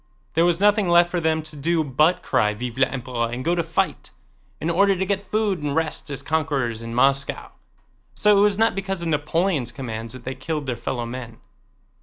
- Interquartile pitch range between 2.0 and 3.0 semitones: No, wide, 5.4 semitones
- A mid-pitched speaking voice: Yes, medium, 155 Hz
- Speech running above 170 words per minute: Yes, fast, 205 wpm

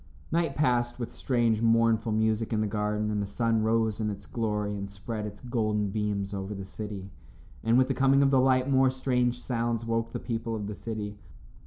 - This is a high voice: No, low, 110 Hz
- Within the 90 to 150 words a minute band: No, fast, 205 wpm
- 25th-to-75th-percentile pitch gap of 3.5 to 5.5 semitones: No, narrow, 2.5 semitones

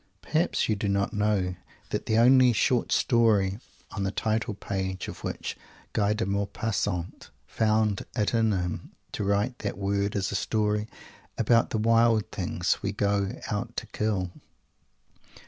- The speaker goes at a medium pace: Yes, average, 150 wpm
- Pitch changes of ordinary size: No, narrow, 2.2 semitones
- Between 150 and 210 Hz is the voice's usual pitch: No, low, 105 Hz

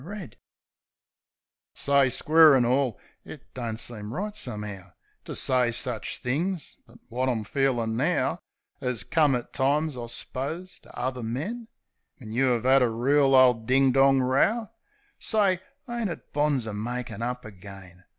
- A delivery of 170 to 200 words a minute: No, average, 160 wpm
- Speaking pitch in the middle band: No, low, 130 Hz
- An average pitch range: Yes, average, 3.9 semitones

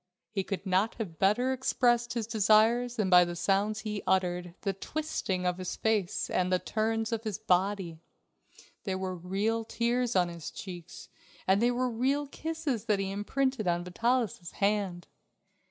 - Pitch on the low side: No, high, 205 Hz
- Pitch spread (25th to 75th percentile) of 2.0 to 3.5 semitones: No, average, 4.2 semitones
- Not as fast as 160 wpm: No, average, 165 wpm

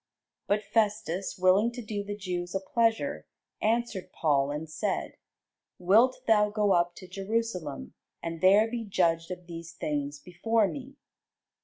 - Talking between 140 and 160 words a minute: Yes, average, 145 wpm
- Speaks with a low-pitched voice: No, high, 190 Hz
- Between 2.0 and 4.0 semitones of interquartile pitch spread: No, average, 4.6 semitones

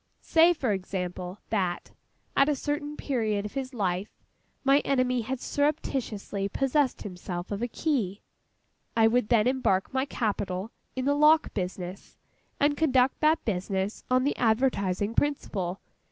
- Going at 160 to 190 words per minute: No, average, 140 wpm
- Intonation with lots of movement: Yes, wide, 5.9 semitones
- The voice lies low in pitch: No, high, 235 Hz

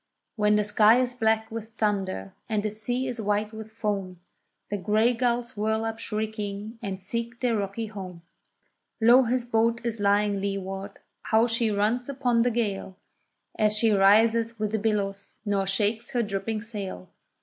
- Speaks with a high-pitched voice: Yes, high, 215 Hz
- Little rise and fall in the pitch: Yes, narrow, 2.3 semitones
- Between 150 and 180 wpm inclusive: Yes, average, 165 wpm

